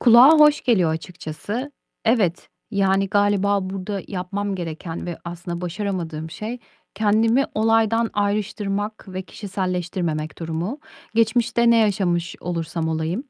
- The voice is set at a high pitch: Yes, high, 195 Hz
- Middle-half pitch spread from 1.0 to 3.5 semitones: No, average, 4.1 semitones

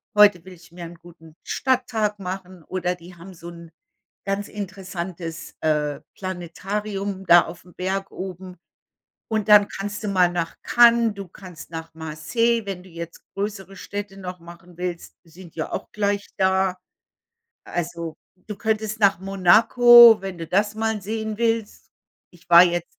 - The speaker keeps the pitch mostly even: No, average, 3.2 semitones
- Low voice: No, high, 190 Hz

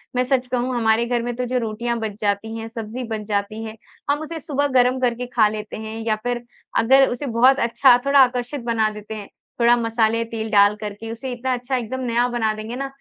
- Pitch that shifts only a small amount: Yes, narrow, 2.3 semitones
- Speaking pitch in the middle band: No, high, 235 Hz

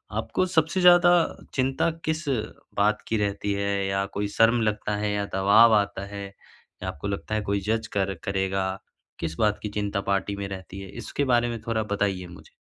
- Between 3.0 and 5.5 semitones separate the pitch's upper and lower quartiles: No, narrow, 2.4 semitones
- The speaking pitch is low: Yes, low, 100 Hz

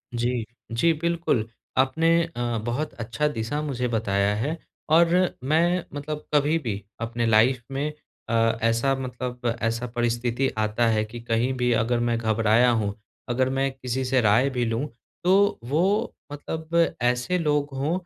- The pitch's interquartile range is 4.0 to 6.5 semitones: Yes, average, 4.4 semitones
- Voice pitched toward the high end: No, low, 125 Hz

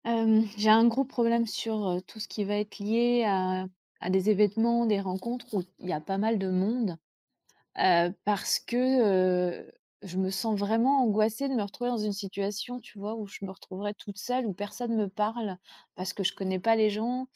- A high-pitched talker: Yes, high, 210 Hz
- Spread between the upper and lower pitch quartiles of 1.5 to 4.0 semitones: Yes, average, 3.1 semitones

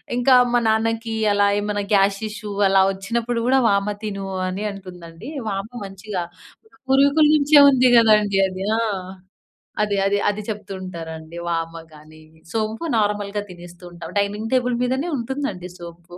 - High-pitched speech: Yes, high, 205 Hz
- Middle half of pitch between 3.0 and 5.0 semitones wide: Yes, average, 3.7 semitones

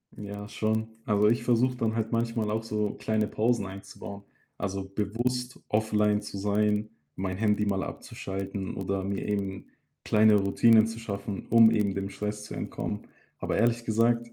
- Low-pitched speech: Yes, low, 105 Hz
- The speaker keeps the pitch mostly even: Yes, narrow, 2.1 semitones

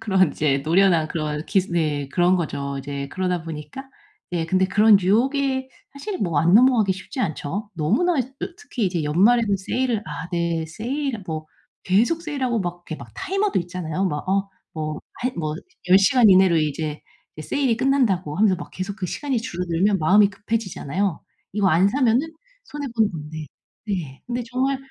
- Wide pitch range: Yes, wide, 6.7 semitones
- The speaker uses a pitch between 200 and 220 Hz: No, high, 190 Hz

